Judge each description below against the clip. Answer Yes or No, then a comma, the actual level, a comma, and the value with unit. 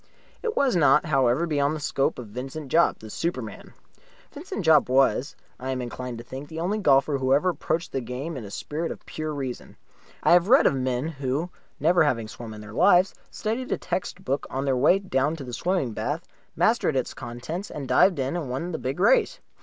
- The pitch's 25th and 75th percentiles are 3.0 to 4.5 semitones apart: No, average, 4.9 semitones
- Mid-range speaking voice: Yes, medium, 145 Hz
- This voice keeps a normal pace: No, fast, 210 wpm